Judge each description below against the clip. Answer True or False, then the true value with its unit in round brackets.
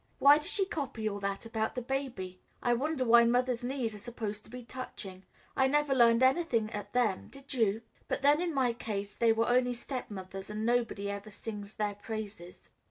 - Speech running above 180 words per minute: True (195 wpm)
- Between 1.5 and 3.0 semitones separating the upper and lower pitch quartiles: False (3.8 semitones)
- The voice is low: False (235 Hz)